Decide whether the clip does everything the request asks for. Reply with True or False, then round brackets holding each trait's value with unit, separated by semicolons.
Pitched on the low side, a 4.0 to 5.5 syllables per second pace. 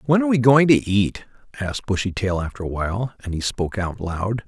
False (110 Hz; 5.9 syllables/s)